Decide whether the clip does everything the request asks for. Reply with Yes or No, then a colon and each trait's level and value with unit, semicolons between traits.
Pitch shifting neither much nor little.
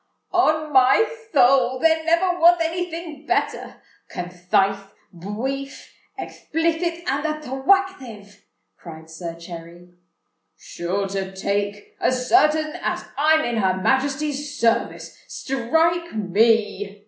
No: wide, 8.2 semitones